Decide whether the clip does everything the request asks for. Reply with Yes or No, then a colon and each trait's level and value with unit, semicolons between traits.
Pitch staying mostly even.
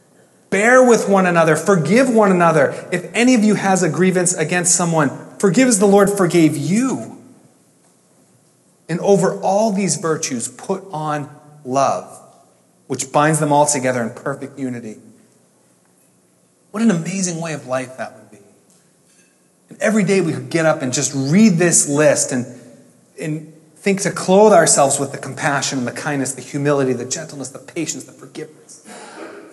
No: wide, 5.6 semitones